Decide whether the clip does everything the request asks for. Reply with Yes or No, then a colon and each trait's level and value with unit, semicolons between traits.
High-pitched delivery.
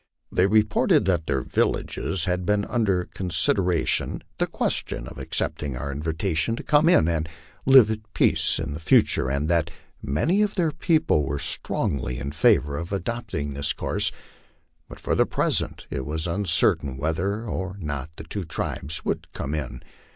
No: very low, 85 Hz